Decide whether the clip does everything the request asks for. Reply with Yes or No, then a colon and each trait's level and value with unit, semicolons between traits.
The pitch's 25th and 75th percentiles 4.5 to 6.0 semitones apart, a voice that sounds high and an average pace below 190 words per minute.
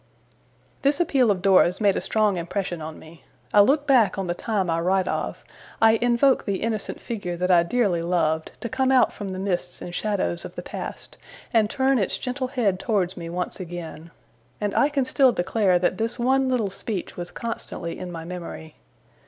No: average, 5.3 semitones; high, 200 Hz; average, 195 wpm